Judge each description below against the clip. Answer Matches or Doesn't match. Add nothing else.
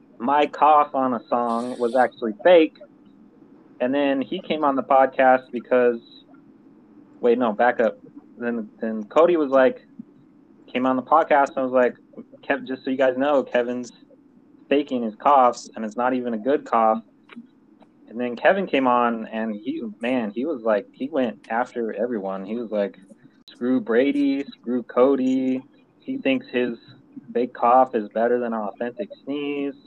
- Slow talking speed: Doesn't match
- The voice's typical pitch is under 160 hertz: Matches